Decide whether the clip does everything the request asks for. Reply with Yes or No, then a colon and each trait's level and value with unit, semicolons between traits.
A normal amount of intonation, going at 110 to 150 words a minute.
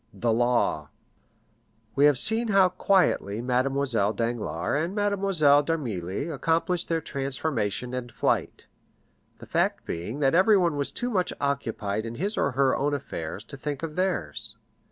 No: wide, 6.3 semitones; average, 145 wpm